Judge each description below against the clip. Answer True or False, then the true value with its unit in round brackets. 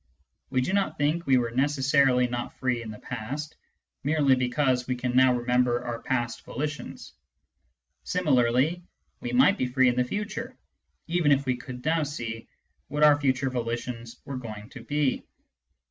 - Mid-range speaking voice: False (130 Hz)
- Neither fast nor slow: True (160 wpm)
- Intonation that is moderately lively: True (3.2 semitones)